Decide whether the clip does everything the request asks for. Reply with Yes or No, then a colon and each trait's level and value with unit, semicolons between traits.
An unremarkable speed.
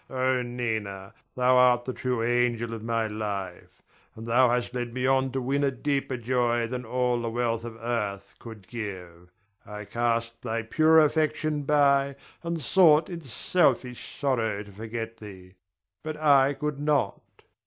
Yes: average, 160 wpm